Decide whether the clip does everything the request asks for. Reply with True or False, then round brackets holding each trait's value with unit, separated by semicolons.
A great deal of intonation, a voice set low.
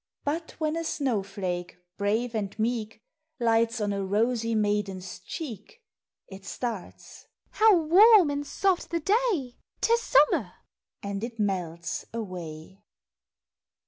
False (7.5 semitones; 225 Hz)